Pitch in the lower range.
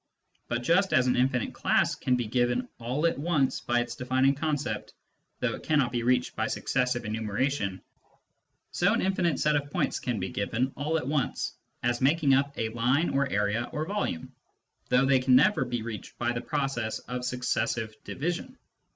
Yes: low, 125 Hz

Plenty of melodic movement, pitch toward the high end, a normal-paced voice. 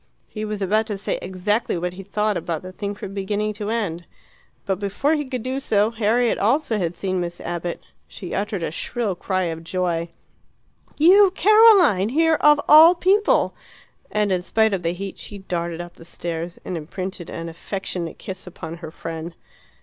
No: average, 4.2 semitones; high, 195 Hz; average, 180 wpm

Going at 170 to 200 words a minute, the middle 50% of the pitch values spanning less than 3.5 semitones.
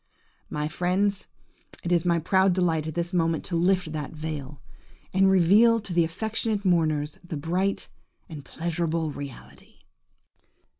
No: average, 140 wpm; average, 3.1 semitones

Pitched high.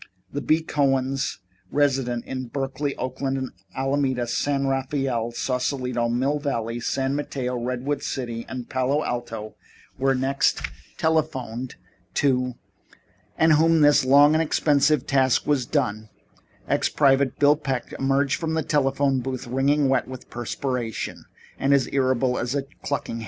No: low, 135 Hz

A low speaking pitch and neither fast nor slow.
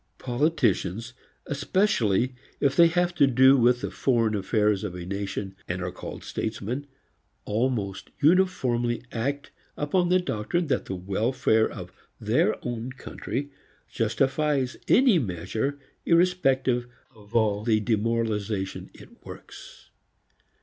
No: low, 120 Hz; slow, 120 wpm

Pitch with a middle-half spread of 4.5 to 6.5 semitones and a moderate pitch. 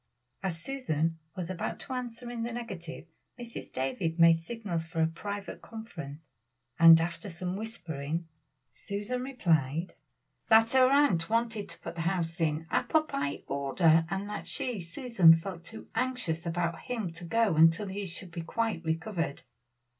Yes: wide, 5.5 semitones; medium, 175 Hz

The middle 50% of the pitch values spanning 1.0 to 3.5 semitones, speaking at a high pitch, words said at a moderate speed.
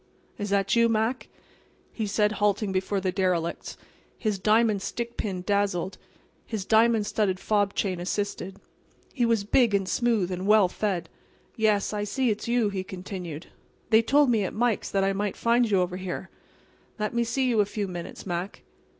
Yes: average, 2.9 semitones; high, 205 Hz; average, 175 wpm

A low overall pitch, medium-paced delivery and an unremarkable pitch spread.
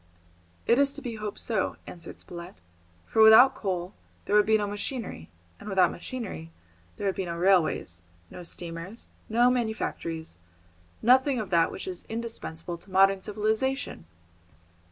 No: high, 205 Hz; average, 150 wpm; average, 4.7 semitones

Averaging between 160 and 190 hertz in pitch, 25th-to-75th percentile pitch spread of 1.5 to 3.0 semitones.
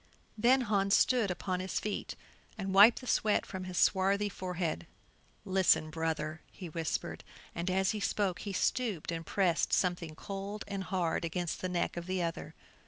Yes: medium, 185 Hz; average, 2.7 semitones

